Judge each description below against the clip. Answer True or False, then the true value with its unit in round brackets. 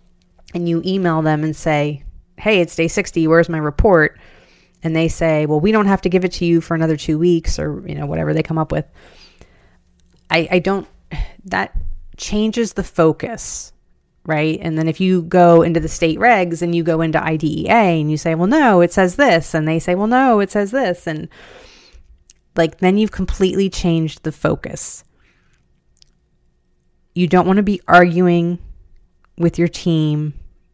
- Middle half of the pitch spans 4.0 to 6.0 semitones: False (2.7 semitones)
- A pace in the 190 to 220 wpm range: False (180 wpm)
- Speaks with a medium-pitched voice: True (165 Hz)